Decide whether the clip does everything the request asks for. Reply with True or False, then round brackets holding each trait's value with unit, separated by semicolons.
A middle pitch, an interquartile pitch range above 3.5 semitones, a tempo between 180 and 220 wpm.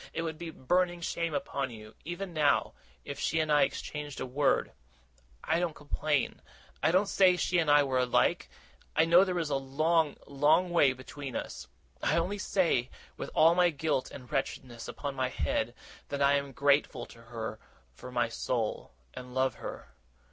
True (145 Hz; 4.3 semitones; 185 wpm)